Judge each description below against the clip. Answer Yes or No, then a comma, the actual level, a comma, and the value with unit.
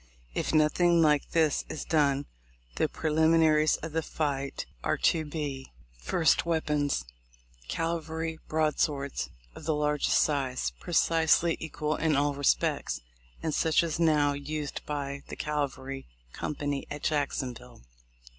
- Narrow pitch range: Yes, narrow, 2.2 semitones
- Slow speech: Yes, slow, 130 wpm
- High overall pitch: No, medium, 150 Hz